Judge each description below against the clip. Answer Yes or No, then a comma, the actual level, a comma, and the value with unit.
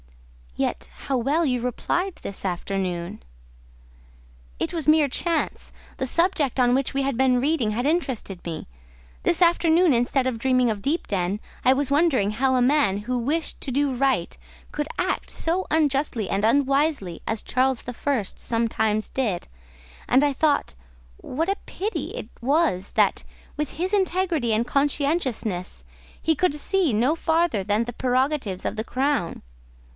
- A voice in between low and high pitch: No, very high, 265 Hz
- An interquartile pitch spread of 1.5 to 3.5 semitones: No, average, 5.3 semitones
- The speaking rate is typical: Yes, average, 155 wpm